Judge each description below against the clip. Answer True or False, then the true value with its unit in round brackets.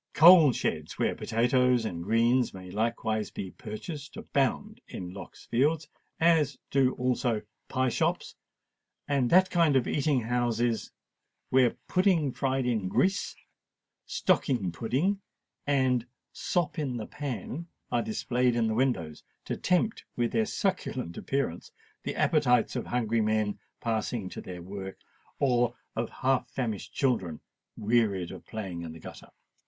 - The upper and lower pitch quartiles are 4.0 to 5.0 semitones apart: True (4.4 semitones)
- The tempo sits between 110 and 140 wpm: True (135 wpm)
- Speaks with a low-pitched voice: True (125 Hz)